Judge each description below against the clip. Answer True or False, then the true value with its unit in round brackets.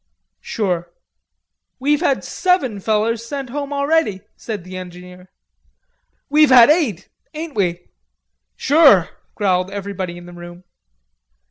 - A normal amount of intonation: False (7.6 semitones)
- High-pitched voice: True (210 Hz)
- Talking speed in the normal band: False (115 wpm)